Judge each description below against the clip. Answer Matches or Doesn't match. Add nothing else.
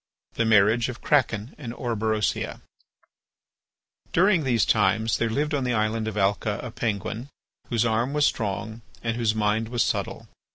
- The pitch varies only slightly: Matches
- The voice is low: Matches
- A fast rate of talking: Doesn't match